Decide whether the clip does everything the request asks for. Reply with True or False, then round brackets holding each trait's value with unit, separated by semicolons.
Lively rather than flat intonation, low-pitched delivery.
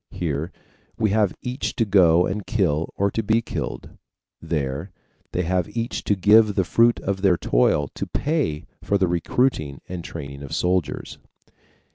False (4.8 semitones; 95 Hz)